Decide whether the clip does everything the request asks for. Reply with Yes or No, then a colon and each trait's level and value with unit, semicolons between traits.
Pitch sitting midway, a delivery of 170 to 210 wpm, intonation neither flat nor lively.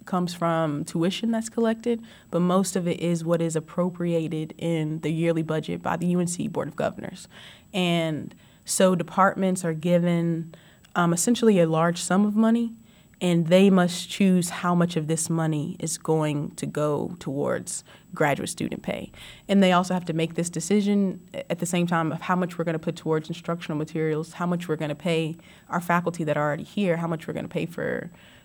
No: medium, 170 Hz; average, 195 wpm; narrow, 2.1 semitones